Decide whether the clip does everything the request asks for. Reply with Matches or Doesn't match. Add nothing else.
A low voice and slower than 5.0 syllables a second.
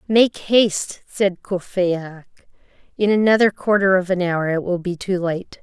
Doesn't match